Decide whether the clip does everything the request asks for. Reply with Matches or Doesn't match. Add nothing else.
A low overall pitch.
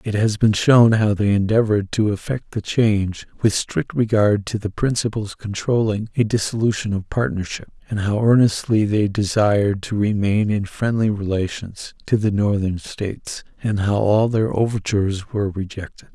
Matches